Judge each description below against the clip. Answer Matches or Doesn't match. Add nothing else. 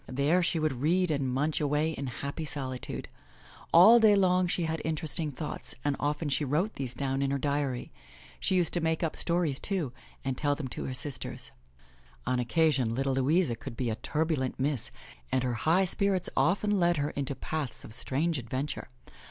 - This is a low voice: Doesn't match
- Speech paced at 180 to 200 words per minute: Matches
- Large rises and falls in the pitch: Doesn't match